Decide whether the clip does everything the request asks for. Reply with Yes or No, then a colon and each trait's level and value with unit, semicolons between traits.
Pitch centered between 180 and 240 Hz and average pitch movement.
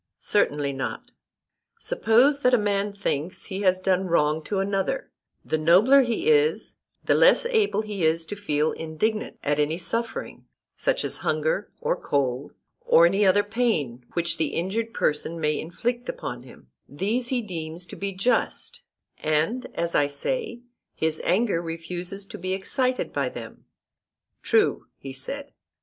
No: high, 190 Hz; wide, 7.0 semitones